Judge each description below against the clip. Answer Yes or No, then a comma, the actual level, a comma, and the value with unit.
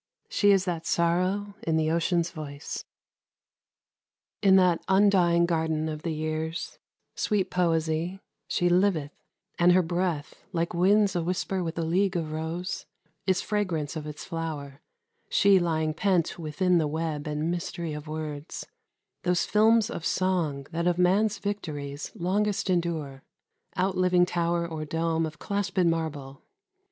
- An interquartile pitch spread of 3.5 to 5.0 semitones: No, average, 2.8 semitones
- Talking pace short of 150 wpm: Yes, average, 140 wpm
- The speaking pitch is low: No, medium, 170 Hz